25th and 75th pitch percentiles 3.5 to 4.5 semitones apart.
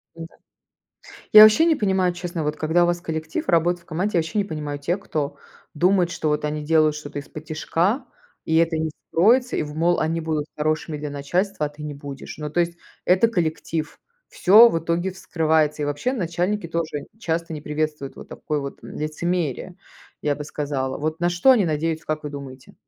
No: average, 2.7 semitones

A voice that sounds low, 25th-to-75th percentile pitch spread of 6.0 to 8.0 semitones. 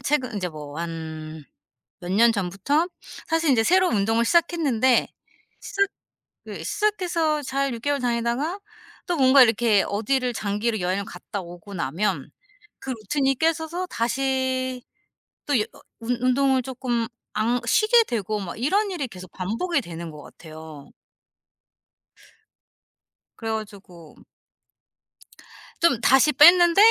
No: high, 240 Hz; wide, 6.5 semitones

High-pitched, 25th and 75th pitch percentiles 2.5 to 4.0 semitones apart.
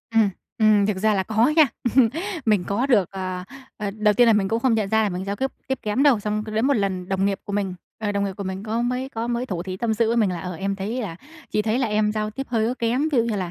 Yes: high, 215 Hz; average, 2.8 semitones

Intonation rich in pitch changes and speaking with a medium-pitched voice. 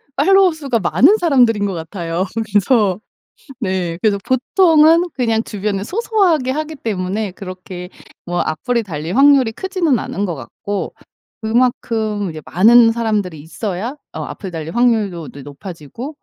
No: wide, 6.1 semitones; high, 215 Hz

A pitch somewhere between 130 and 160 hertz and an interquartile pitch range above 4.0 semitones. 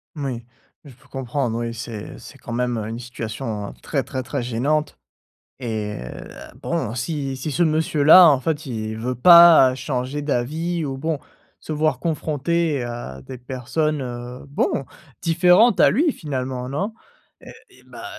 Yes: low, 135 Hz; average, 4.4 semitones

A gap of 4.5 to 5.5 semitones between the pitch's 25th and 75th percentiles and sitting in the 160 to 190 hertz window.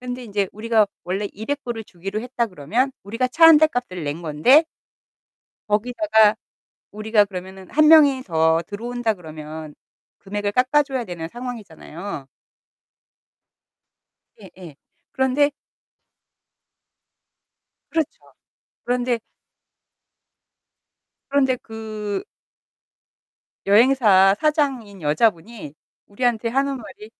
No: average, 5.1 semitones; high, 220 Hz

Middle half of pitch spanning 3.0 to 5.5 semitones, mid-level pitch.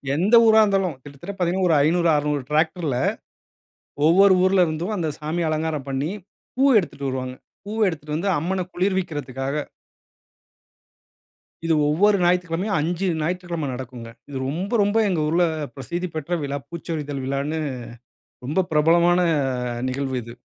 Yes: average, 4.0 semitones; medium, 165 Hz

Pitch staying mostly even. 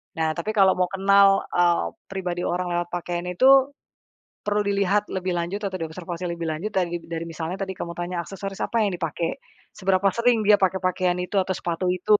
Yes: narrow, 2.3 semitones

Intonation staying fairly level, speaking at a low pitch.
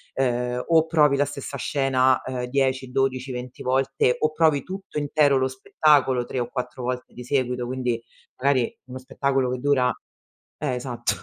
Yes: narrow, 2.0 semitones; low, 130 Hz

